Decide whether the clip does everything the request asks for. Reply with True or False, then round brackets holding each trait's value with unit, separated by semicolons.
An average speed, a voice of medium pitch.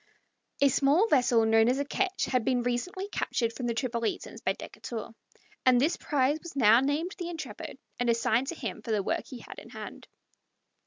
False (195 wpm; 255 Hz)